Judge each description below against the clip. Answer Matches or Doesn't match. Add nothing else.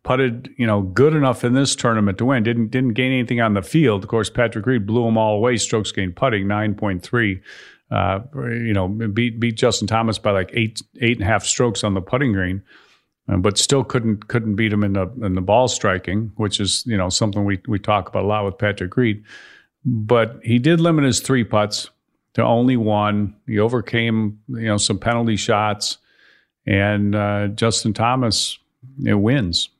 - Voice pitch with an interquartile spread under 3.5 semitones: Matches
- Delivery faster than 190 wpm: Matches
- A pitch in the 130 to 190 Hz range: Doesn't match